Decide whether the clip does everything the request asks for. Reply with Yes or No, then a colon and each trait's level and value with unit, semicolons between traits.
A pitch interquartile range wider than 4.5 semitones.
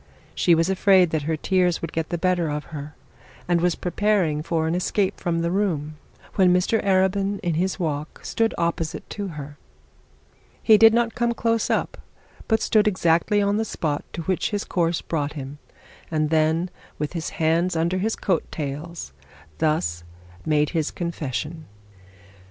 No: average, 3.6 semitones